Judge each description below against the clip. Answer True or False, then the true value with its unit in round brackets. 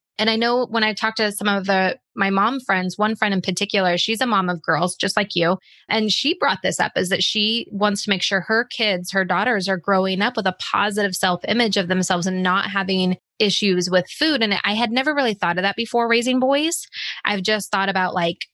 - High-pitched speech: True (200 Hz)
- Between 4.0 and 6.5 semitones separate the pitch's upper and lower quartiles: False (2.8 semitones)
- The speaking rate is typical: False (235 wpm)